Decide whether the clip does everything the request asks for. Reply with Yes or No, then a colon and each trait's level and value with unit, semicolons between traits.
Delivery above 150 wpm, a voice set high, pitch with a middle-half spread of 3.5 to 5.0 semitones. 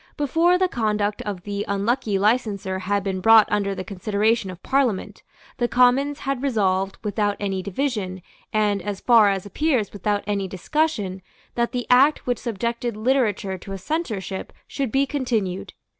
Yes: average, 160 wpm; high, 210 Hz; average, 4.2 semitones